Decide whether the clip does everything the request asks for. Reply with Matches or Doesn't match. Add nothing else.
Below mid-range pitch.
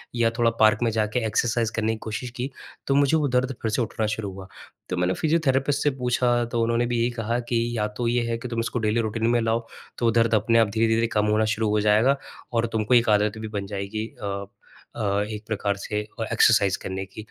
Matches